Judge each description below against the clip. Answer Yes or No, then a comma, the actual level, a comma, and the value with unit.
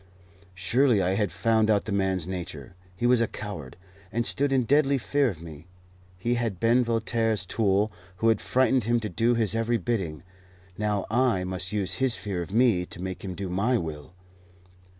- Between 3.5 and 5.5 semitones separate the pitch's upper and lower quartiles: Yes, average, 4.3 semitones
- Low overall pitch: Yes, low, 105 Hz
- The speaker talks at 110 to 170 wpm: No, average, 190 wpm